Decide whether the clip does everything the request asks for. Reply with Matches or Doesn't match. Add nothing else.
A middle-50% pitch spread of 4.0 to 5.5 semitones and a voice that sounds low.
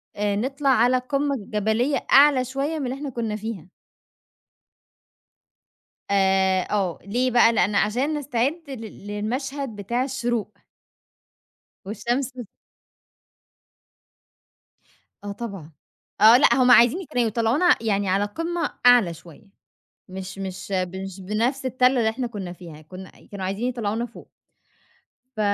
Doesn't match